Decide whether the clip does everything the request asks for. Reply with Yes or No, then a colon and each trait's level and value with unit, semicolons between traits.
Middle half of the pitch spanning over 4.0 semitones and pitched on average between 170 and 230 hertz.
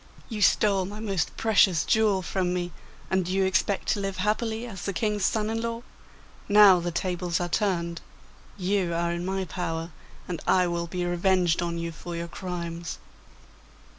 No: average, 2.9 semitones; medium, 185 Hz